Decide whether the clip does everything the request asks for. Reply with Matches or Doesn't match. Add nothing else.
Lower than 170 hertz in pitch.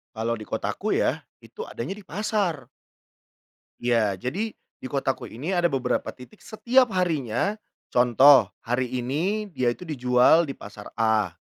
Matches